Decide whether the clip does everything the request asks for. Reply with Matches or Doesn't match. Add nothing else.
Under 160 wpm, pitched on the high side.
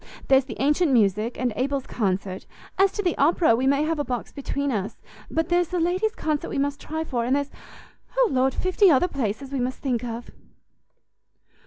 Doesn't match